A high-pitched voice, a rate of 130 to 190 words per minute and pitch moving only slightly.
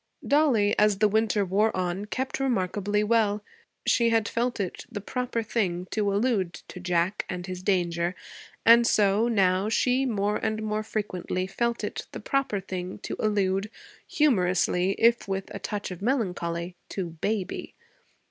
No: high, 205 Hz; average, 155 wpm; average, 3.5 semitones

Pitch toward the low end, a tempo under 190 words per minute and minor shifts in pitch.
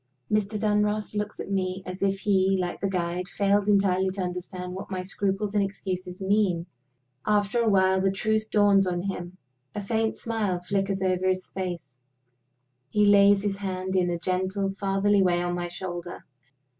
No: high, 195 Hz; average, 170 wpm; narrow, 1.8 semitones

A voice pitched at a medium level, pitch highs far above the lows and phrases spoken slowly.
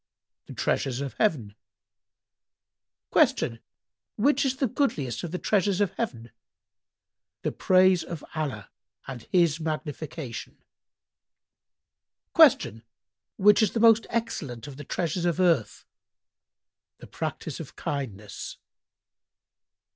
Yes: medium, 160 Hz; wide, 7.4 semitones; slow, 100 wpm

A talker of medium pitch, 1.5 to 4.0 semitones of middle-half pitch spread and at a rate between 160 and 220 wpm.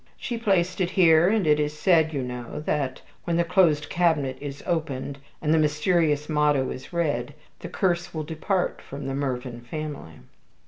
Yes: medium, 155 Hz; average, 3.4 semitones; average, 175 wpm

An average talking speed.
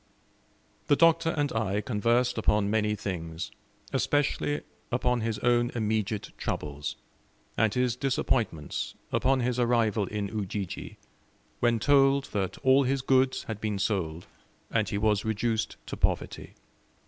No: slow, 130 wpm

